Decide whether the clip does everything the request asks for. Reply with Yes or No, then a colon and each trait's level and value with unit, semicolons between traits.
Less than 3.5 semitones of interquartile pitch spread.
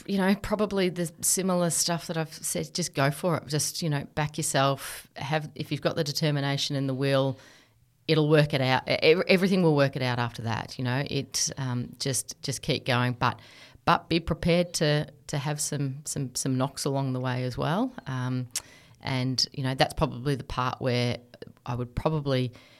No: average, 3.8 semitones